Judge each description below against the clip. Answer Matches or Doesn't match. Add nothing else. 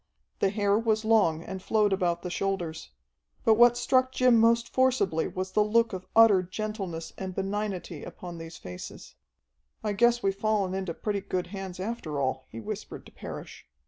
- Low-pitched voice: Doesn't match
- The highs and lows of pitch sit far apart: Doesn't match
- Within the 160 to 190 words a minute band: Matches